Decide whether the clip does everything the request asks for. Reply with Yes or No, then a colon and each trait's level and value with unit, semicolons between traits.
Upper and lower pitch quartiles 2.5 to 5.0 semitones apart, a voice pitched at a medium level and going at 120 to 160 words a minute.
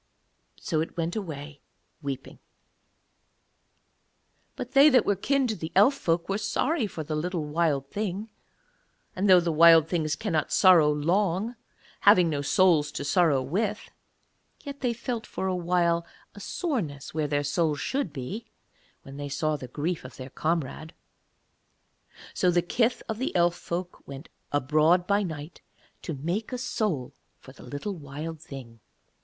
No: wide, 5.4 semitones; medium, 170 Hz; average, 155 wpm